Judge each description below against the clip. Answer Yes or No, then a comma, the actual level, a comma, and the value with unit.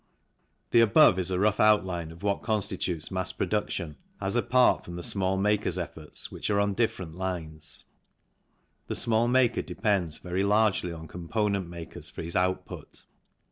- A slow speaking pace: No, average, 155 wpm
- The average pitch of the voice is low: Yes, very low, 95 Hz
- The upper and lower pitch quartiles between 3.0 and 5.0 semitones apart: Yes, average, 3.4 semitones